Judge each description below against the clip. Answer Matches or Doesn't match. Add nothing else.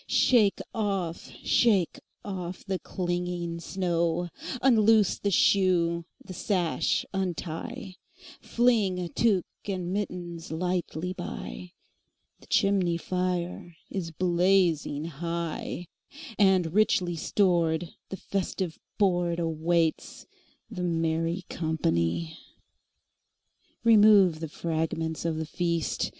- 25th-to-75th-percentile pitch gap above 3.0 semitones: Doesn't match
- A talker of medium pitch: Matches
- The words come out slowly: Matches